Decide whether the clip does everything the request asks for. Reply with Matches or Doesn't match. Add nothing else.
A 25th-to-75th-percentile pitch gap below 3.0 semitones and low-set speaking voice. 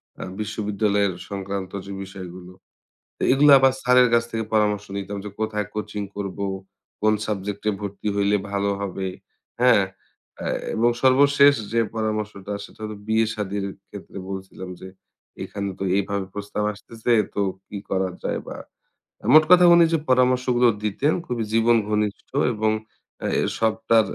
Matches